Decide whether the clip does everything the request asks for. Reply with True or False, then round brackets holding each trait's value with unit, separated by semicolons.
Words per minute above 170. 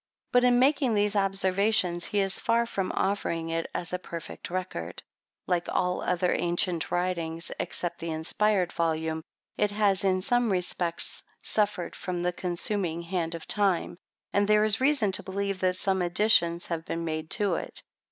False (165 wpm)